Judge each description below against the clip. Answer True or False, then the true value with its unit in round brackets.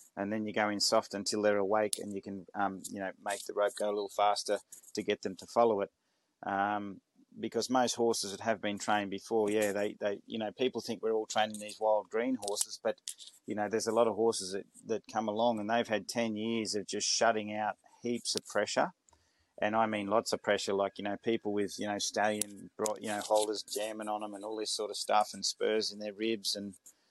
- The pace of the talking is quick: True (240 wpm)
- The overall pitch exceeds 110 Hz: False (105 Hz)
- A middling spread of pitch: False (1.4 semitones)